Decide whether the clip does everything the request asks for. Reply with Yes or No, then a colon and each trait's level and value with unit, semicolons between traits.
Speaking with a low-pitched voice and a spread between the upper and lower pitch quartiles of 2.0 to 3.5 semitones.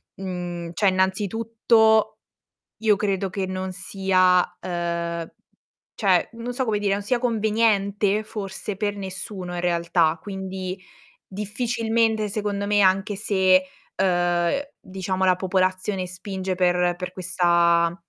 No: high, 190 Hz; narrow, 2.5 semitones